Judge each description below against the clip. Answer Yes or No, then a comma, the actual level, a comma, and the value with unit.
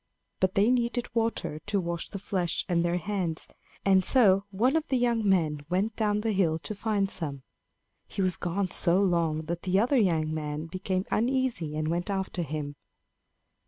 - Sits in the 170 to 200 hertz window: Yes, high, 190 Hz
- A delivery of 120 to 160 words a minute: No, average, 180 wpm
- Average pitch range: Yes, average, 4.1 semitones